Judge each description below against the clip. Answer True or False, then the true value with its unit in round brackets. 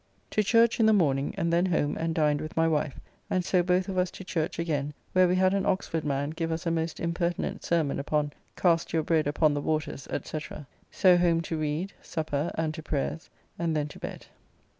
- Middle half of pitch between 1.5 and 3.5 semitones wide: True (2.8 semitones)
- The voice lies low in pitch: False (165 Hz)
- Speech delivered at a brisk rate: True (215 wpm)